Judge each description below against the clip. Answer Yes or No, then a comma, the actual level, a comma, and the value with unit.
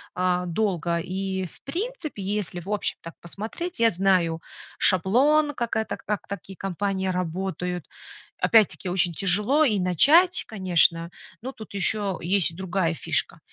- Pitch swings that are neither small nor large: Yes, average, 3.7 semitones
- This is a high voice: Yes, high, 195 Hz